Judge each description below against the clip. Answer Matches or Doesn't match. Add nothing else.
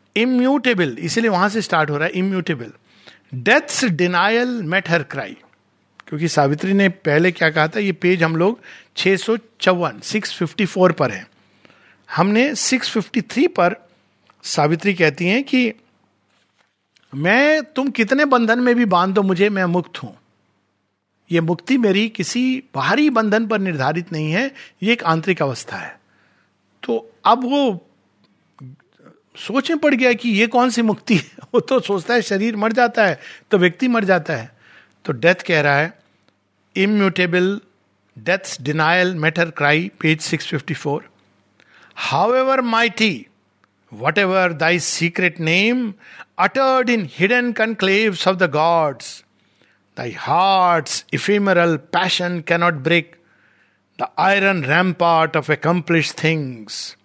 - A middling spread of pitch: Doesn't match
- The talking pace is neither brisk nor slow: Matches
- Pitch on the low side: Doesn't match